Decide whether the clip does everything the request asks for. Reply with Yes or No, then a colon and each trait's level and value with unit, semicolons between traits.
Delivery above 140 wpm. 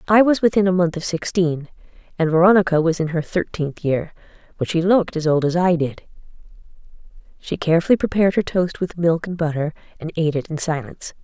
Yes: average, 190 wpm